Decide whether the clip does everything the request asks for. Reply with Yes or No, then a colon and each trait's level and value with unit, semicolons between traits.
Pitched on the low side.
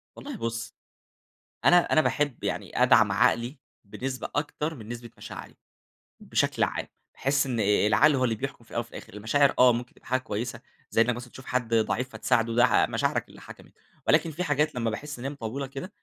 Yes: low, 125 Hz